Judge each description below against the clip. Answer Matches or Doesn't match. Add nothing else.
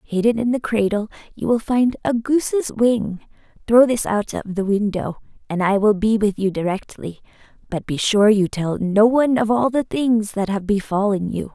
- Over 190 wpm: Matches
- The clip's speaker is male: Doesn't match